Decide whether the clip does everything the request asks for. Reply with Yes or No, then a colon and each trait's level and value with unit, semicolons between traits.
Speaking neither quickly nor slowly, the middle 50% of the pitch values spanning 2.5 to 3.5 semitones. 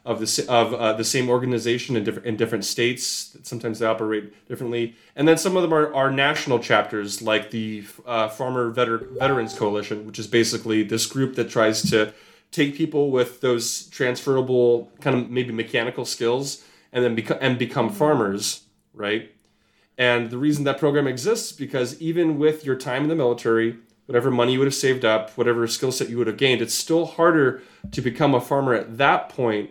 Yes: average, 195 wpm; average, 3.2 semitones